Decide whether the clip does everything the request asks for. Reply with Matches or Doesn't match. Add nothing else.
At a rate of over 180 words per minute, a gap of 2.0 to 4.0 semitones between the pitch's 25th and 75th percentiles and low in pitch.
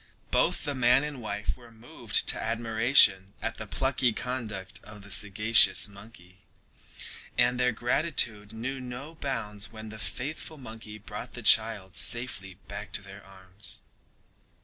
Doesn't match